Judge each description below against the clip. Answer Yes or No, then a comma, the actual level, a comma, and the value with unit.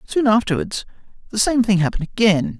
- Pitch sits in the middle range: No, high, 205 Hz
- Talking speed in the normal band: Yes, average, 160 wpm